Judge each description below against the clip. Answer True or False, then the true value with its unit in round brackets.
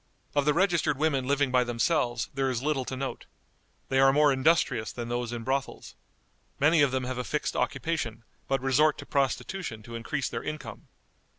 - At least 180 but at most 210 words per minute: True (185 wpm)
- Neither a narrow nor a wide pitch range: True (3.3 semitones)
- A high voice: False (135 Hz)